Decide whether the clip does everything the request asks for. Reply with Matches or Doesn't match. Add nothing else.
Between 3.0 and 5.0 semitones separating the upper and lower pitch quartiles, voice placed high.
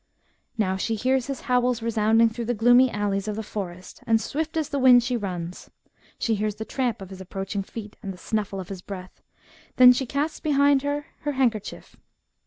Matches